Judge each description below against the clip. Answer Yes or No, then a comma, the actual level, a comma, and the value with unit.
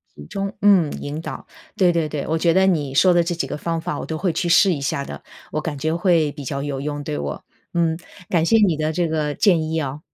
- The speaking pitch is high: No, medium, 160 Hz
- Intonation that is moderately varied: Yes, average, 3.0 semitones